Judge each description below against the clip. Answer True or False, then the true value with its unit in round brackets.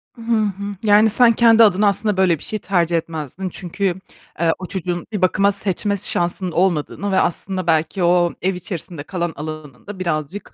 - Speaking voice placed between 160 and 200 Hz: True (185 Hz)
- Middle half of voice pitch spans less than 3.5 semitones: True (3.1 semitones)